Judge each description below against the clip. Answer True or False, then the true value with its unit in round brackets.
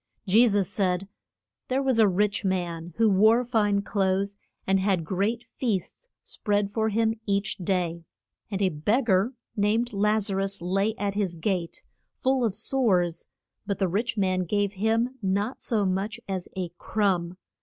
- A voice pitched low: False (200 Hz)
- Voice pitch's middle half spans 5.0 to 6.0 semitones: False (2.7 semitones)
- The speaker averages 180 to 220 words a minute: False (165 wpm)